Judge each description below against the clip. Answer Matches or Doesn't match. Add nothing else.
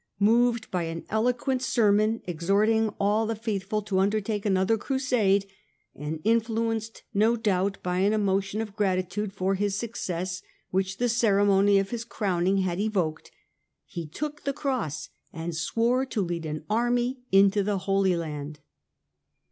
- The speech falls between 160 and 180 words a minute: Doesn't match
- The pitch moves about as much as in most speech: Matches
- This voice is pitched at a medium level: Doesn't match